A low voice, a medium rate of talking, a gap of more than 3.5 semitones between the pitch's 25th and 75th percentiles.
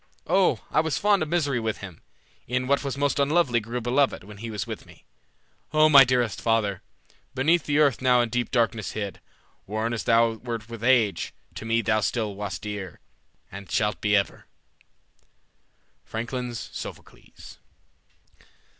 Yes: low, 115 Hz; average, 160 wpm; average, 4.2 semitones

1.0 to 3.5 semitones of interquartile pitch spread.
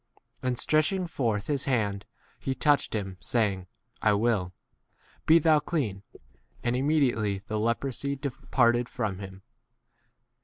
No: average, 5.3 semitones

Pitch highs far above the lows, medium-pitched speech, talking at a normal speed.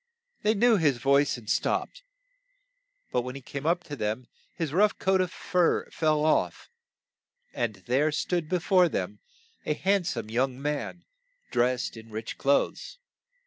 Yes: wide, 5.9 semitones; medium, 150 Hz; average, 155 wpm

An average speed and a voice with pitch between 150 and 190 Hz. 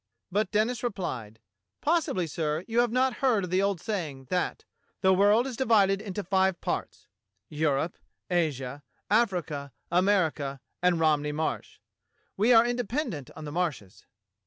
Yes: average, 145 wpm; medium, 185 Hz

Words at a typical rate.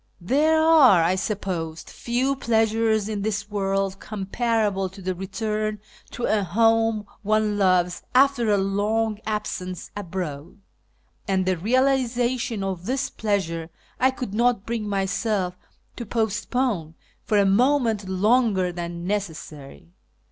No: slow, 125 wpm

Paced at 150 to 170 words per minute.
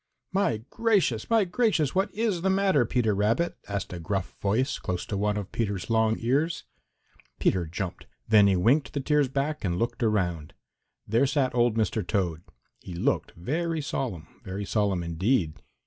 Yes: average, 165 wpm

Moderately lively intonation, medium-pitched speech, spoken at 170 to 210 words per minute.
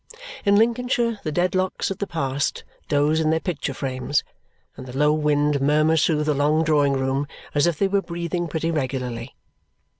Yes: average, 3.4 semitones; medium, 155 Hz; average, 175 wpm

